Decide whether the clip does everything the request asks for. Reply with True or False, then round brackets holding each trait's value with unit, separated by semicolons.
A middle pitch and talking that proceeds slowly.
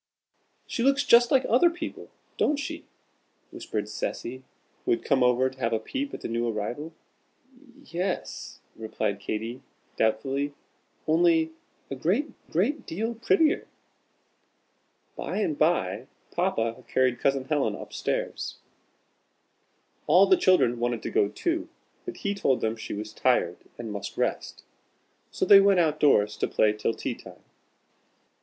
False (145 Hz; 150 wpm)